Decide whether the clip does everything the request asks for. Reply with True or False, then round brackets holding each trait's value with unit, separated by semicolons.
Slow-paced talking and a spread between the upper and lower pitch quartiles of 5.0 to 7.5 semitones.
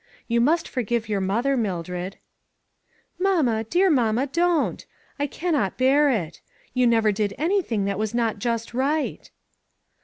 False (145 wpm; 5.5 semitones)